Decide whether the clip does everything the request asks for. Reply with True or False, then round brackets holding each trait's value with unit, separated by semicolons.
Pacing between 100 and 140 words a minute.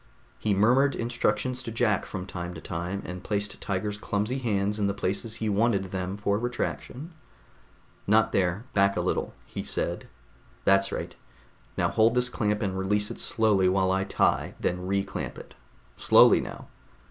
False (165 wpm)